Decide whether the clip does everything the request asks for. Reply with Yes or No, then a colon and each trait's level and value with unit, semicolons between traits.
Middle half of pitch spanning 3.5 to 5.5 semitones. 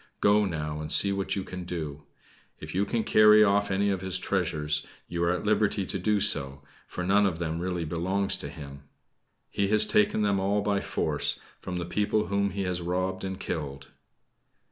No: average, 3.0 semitones